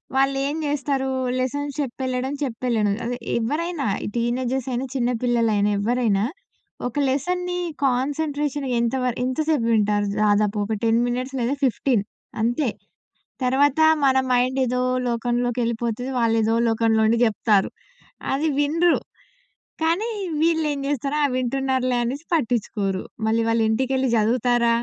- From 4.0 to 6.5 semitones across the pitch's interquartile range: No, average, 3.2 semitones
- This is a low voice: No, very high, 250 Hz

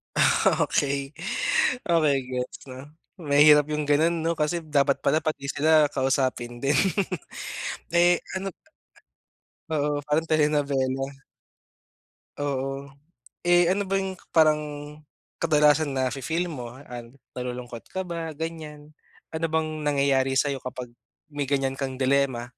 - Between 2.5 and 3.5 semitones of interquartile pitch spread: Yes, average, 2.9 semitones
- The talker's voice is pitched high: No, medium, 145 Hz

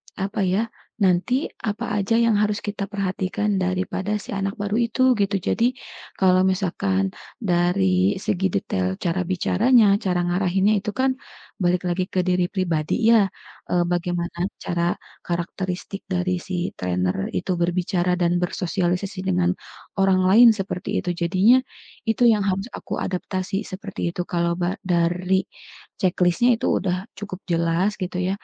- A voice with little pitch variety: Yes, narrow, 2.2 semitones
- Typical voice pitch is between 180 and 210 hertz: Yes, medium, 185 Hz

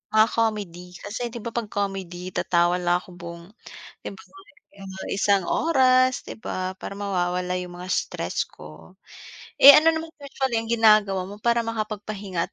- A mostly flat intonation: No, average, 4.2 semitones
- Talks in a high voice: Yes, high, 200 Hz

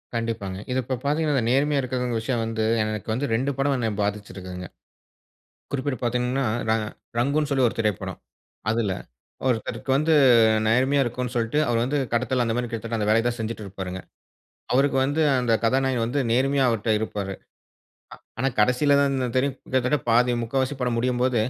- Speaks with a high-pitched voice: No, low, 125 Hz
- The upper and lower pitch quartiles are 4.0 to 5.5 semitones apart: No, average, 3.0 semitones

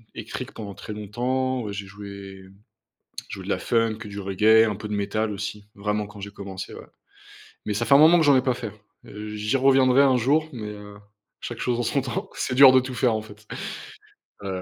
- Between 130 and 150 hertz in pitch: No, low, 110 Hz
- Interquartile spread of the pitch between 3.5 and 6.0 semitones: Yes, average, 3.8 semitones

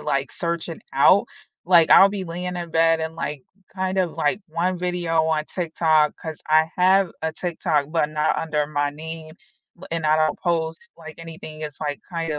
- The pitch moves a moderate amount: No, narrow, 2.0 semitones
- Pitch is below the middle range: No, medium, 160 Hz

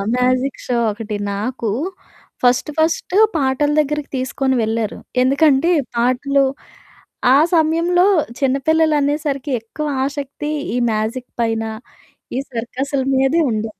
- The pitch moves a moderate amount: Yes, average, 3.3 semitones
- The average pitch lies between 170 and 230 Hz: No, very high, 270 Hz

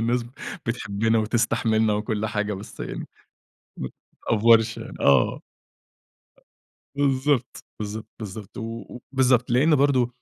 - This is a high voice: No, low, 115 Hz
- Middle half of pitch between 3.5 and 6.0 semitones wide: No, narrow, 2.5 semitones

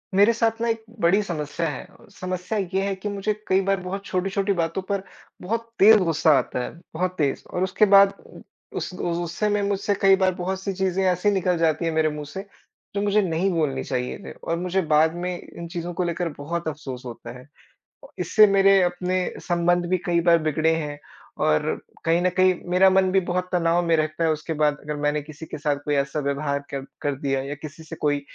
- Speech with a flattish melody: No, average, 3.8 semitones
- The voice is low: No, medium, 175 Hz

